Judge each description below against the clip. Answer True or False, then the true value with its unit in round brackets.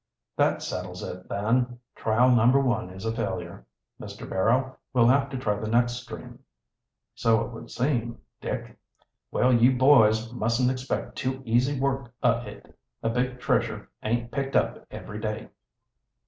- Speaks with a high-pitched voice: False (120 Hz)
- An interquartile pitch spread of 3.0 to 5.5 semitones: False (2.5 semitones)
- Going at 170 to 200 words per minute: False (155 wpm)